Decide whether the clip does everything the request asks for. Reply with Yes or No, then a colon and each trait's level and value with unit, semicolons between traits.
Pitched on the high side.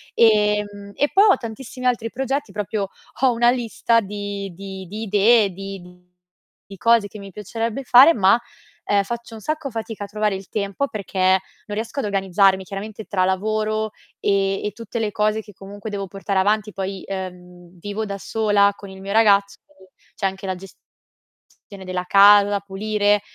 Yes: high, 205 Hz